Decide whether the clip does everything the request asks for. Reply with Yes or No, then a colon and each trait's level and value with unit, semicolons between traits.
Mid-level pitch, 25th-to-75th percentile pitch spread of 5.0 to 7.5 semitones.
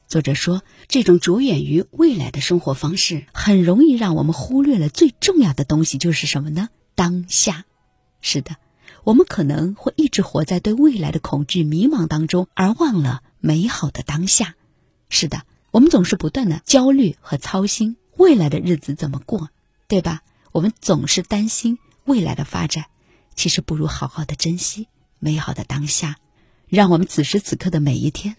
Yes: medium, 175 Hz; wide, 5.4 semitones